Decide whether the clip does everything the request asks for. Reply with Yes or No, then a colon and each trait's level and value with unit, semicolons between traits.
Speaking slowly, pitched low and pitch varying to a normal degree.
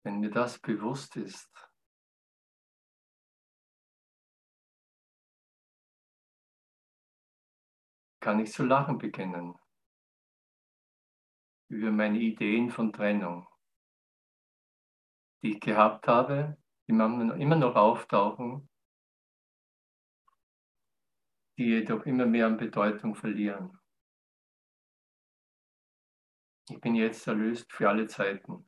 No: slow, 75 wpm; low, 110 Hz; narrow, 2.1 semitones